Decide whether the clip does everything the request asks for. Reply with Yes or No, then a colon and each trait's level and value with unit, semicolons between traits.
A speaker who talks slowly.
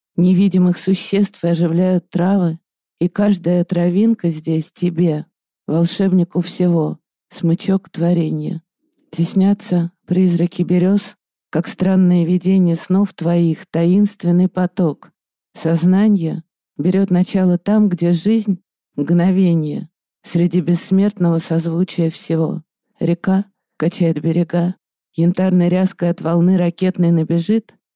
Yes: slow, 95 wpm